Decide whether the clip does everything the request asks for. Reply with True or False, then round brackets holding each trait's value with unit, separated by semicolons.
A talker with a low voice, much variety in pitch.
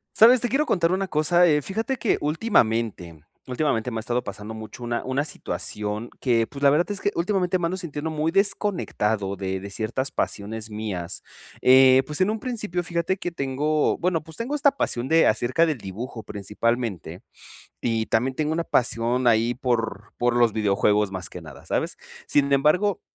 True (130 Hz; 7.4 semitones)